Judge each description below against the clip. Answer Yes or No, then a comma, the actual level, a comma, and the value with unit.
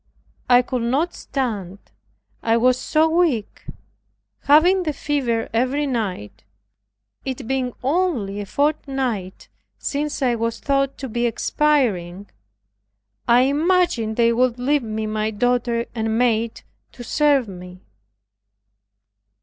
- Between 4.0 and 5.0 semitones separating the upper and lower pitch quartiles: Yes, average, 4.3 semitones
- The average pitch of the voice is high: Yes, high, 245 Hz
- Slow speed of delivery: Yes, slow, 115 wpm